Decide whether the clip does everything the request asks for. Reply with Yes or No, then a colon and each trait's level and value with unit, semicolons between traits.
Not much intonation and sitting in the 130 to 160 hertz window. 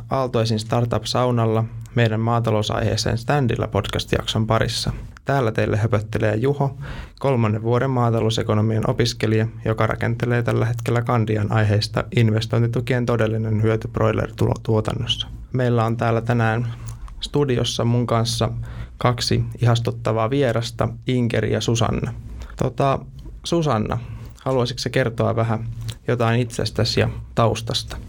No: narrow, 1.6 semitones; low, 115 Hz